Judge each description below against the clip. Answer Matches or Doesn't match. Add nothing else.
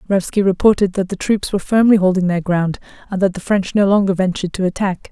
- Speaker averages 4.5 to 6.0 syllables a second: Doesn't match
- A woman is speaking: Matches